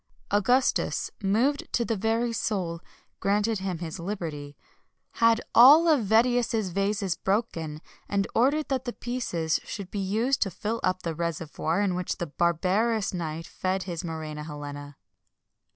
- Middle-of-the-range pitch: No, high, 195 Hz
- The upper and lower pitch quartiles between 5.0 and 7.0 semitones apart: Yes, average, 5.3 semitones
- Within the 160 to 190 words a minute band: No, average, 145 wpm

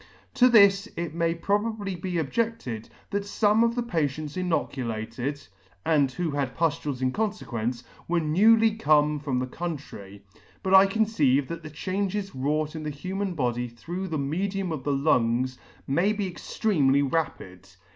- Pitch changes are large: Yes, wide, 6.3 semitones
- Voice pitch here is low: No, medium, 160 Hz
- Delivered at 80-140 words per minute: No, average, 155 wpm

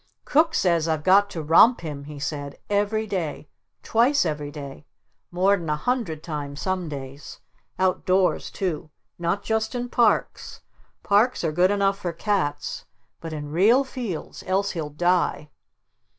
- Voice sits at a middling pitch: Yes, medium, 175 Hz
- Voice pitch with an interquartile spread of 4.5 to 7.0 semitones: Yes, average, 5.1 semitones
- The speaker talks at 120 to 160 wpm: Yes, average, 150 wpm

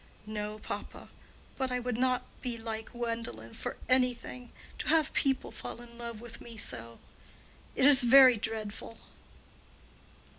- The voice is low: No, high, 235 Hz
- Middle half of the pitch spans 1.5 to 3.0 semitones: Yes, narrow, 2.5 semitones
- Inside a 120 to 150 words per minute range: Yes, average, 140 wpm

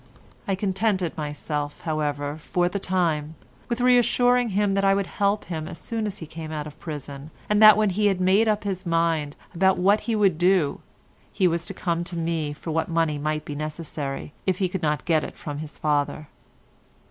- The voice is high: No, medium, 170 Hz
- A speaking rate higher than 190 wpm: Yes, average, 200 wpm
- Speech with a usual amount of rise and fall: Yes, average, 4.5 semitones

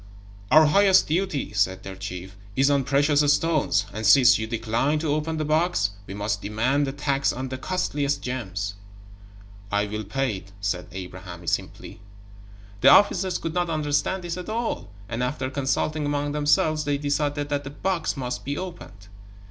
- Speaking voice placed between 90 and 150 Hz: Yes, medium, 140 Hz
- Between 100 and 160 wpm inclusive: No, average, 170 wpm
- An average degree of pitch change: No, wide, 6.1 semitones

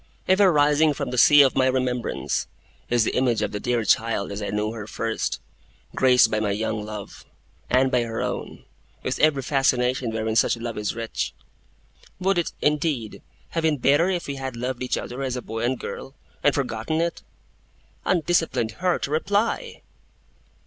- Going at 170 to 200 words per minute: Yes, average, 175 wpm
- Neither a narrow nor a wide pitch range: Yes, average, 4.7 semitones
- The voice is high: No, low, 130 Hz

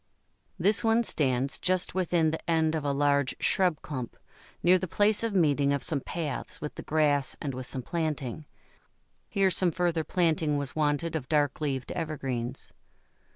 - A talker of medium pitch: Yes, medium, 155 Hz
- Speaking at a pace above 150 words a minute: Yes, average, 165 wpm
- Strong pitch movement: No, average, 3.6 semitones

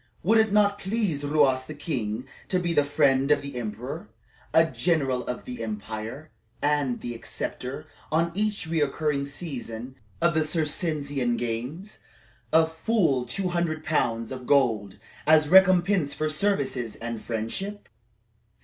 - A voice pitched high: No, medium, 145 Hz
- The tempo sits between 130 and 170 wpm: Yes, average, 140 wpm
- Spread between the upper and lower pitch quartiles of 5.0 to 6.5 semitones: Yes, average, 5.3 semitones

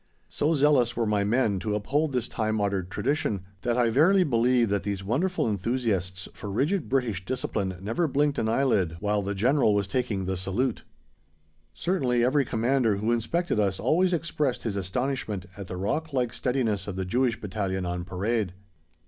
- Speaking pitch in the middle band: No, low, 115 Hz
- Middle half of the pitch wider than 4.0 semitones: Yes, average, 5.0 semitones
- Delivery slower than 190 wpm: Yes, average, 175 wpm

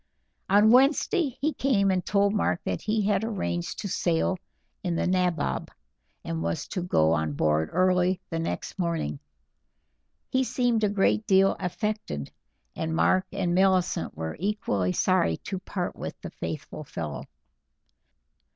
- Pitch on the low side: No, medium, 185 Hz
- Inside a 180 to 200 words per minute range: No, average, 145 wpm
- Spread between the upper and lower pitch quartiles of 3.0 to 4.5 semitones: Yes, average, 4.2 semitones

